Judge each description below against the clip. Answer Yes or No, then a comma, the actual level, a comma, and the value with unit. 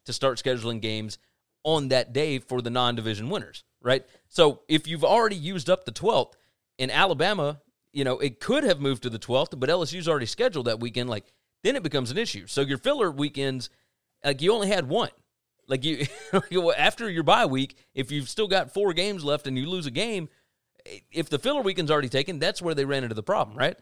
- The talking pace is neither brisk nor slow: No, fast, 215 wpm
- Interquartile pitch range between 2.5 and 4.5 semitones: No, average, 5.1 semitones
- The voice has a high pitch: No, medium, 140 Hz